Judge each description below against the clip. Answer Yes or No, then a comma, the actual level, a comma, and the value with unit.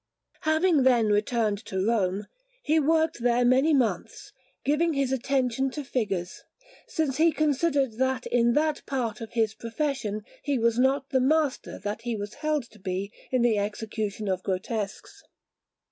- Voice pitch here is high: Yes, high, 245 Hz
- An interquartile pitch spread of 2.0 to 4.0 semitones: No, average, 4.7 semitones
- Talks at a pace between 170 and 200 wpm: No, average, 155 wpm